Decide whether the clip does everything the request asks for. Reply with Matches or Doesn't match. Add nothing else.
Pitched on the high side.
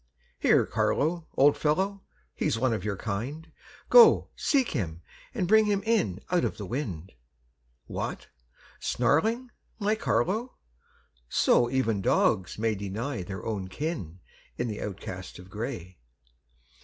Doesn't match